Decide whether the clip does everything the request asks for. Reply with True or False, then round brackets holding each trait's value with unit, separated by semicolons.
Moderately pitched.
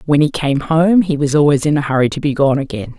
True (145 Hz)